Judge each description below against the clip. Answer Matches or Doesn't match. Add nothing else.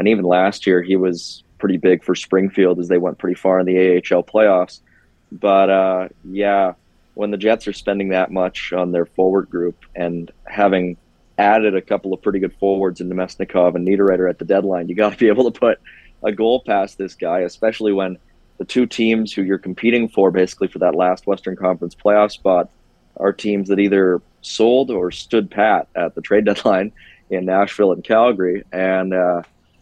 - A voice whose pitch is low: Matches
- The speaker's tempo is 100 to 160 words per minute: Doesn't match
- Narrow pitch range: Matches